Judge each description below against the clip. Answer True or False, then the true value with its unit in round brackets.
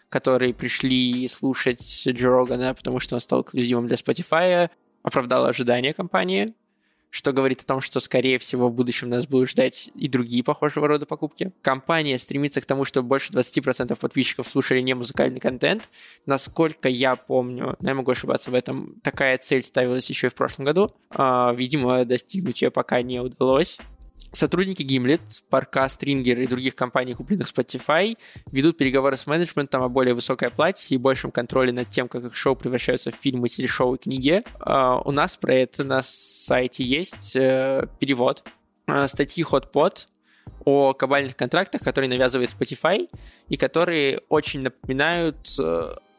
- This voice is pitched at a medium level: False (130 Hz)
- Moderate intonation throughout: False (2.1 semitones)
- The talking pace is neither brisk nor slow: True (150 wpm)